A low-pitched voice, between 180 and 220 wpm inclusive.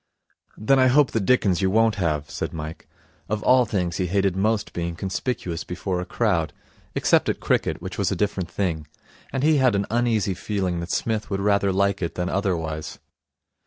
Yes: low, 100 Hz; average, 190 wpm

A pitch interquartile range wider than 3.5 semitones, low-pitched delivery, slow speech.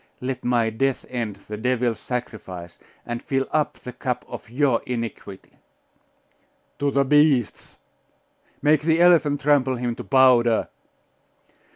No: average, 3.1 semitones; low, 125 Hz; slow, 130 wpm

